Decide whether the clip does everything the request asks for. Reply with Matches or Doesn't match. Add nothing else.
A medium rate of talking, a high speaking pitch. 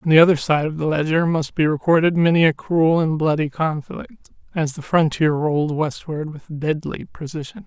Doesn't match